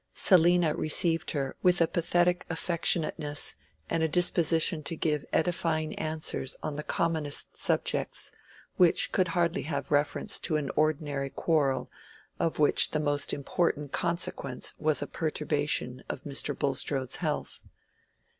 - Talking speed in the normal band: No, slow, 130 wpm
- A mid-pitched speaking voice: Yes, medium, 155 Hz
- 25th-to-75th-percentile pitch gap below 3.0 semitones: Yes, narrow, 2.5 semitones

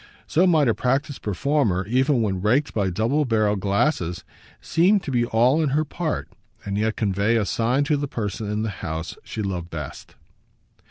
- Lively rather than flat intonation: Yes, wide, 6.1 semitones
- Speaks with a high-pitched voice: No, low, 115 Hz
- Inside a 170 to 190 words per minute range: Yes, average, 180 wpm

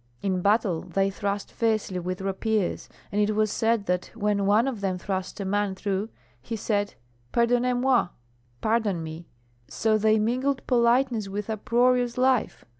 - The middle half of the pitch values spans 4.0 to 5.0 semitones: No, average, 3.1 semitones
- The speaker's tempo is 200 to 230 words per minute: No, average, 155 wpm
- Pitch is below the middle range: No, high, 210 Hz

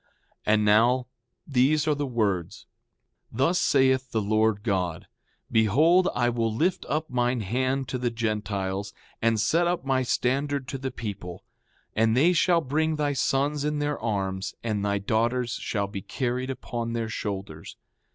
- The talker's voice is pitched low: Yes, low, 120 Hz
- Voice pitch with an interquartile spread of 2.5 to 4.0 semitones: No, average, 4.5 semitones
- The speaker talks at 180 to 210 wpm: No, average, 160 wpm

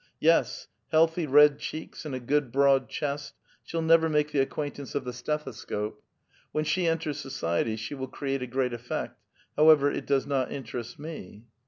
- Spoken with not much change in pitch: No, average, 3.0 semitones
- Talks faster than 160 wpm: Yes, average, 175 wpm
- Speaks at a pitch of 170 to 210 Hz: No, medium, 140 Hz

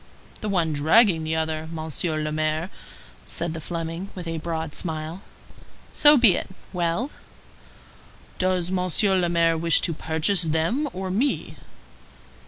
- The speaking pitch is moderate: Yes, medium, 170 Hz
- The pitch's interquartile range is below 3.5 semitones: Yes, average, 2.7 semitones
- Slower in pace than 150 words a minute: Yes, average, 140 wpm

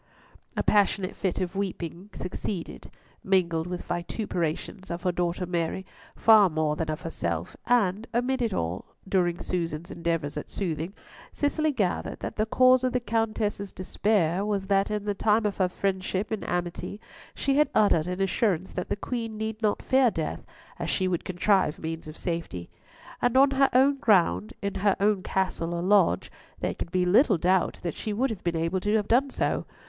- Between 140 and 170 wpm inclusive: No, average, 185 wpm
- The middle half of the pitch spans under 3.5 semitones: No, average, 3.9 semitones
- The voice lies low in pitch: No, high, 190 Hz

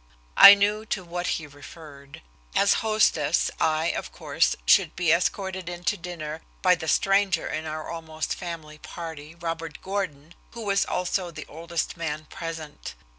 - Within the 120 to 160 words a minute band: Yes, average, 155 wpm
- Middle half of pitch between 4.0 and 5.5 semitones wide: No, average, 2.8 semitones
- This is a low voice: No, medium, 165 Hz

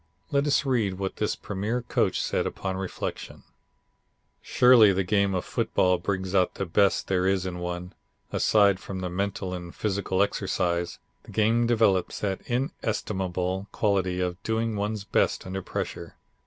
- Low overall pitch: Yes, very low, 95 Hz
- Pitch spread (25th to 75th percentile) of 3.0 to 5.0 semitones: No, narrow, 2.6 semitones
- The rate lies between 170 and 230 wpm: No, average, 155 wpm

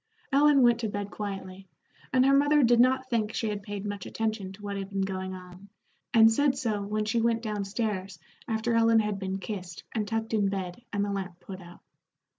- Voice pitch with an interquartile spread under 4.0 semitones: Yes, average, 2.8 semitones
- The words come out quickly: Yes, fast, 215 wpm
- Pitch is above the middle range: Yes, high, 210 Hz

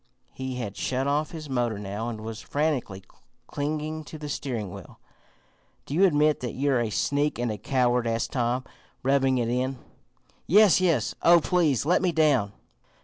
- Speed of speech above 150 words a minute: Yes, average, 170 wpm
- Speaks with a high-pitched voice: No, low, 135 Hz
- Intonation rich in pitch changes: No, average, 4.2 semitones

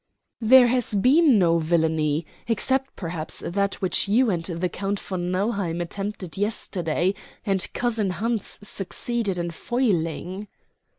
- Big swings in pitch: No, average, 4.8 semitones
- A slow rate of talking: Yes, slow, 125 wpm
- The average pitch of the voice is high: Yes, high, 195 Hz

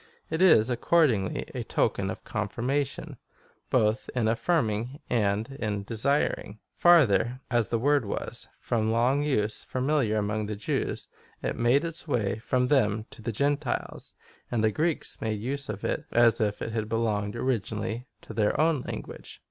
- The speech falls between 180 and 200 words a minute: No, average, 165 wpm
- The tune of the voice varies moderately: Yes, average, 4.3 semitones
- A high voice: No, low, 115 Hz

